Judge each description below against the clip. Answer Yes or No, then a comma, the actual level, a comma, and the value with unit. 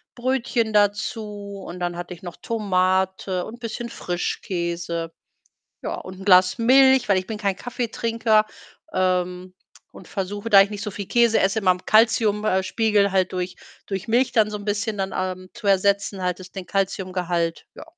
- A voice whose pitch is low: No, high, 200 Hz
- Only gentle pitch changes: No, average, 3.0 semitones